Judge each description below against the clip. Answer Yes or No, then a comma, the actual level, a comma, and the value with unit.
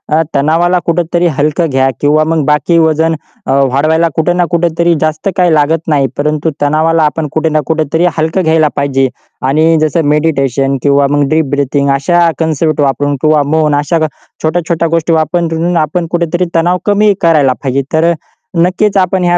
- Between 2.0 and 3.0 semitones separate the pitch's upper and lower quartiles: Yes, narrow, 2.5 semitones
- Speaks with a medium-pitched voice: Yes, medium, 160 Hz